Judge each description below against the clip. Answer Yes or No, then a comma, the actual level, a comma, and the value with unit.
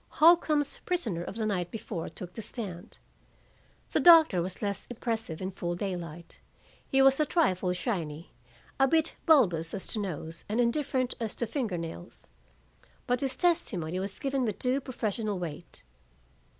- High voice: Yes, high, 215 Hz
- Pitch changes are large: Yes, wide, 7.0 semitones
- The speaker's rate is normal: Yes, average, 155 wpm